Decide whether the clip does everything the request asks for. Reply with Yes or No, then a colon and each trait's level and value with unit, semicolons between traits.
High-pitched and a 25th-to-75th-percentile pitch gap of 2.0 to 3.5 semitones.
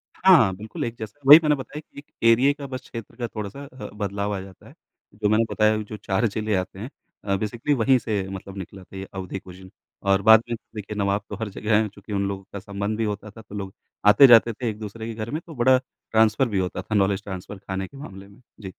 No: low, 105 Hz; average, 2.8 semitones